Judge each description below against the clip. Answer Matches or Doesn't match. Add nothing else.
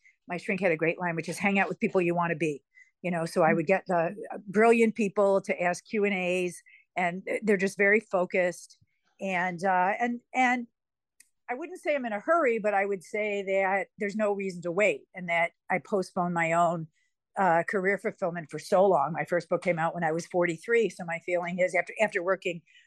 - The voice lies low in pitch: Doesn't match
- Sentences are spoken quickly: Matches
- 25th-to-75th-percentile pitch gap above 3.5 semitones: Doesn't match